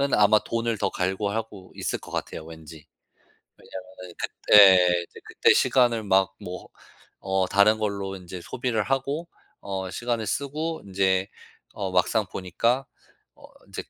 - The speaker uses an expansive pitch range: No, average, 3.6 semitones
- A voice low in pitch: Yes, low, 100 Hz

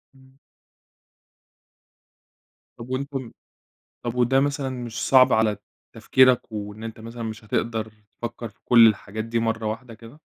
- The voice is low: Yes, low, 115 Hz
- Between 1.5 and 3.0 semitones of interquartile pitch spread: Yes, average, 2.7 semitones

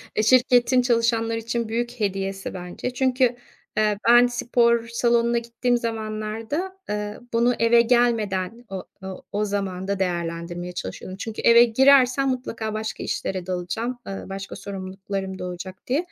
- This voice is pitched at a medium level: No, high, 225 Hz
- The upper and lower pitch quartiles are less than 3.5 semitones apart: No, average, 3.8 semitones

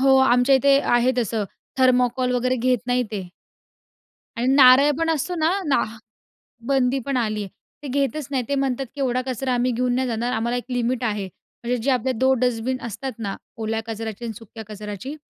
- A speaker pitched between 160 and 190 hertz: No, very high, 250 Hz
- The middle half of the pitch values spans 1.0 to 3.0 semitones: Yes, narrow, 2.5 semitones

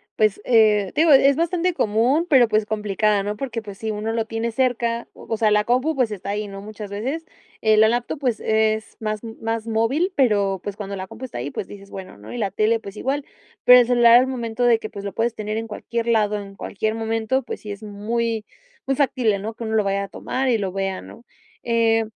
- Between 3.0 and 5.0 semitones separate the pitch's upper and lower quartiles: No, narrow, 2.5 semitones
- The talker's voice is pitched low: No, high, 220 Hz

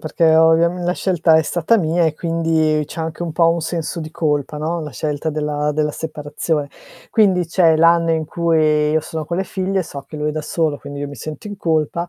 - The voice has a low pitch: No, medium, 160 Hz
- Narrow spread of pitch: Yes, narrow, 1.9 semitones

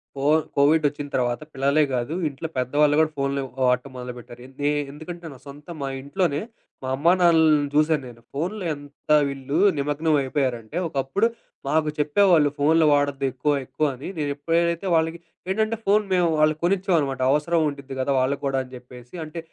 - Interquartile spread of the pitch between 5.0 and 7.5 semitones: No, average, 2.9 semitones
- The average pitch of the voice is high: No, medium, 145 Hz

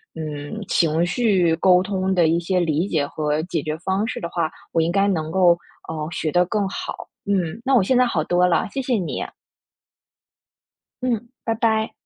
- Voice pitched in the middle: Yes, medium, 180 Hz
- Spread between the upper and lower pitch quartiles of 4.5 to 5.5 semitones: No, average, 4.0 semitones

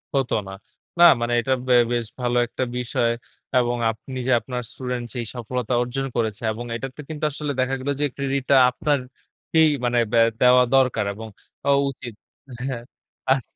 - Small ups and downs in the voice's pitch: Yes, narrow, 2.0 semitones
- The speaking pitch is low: Yes, low, 125 Hz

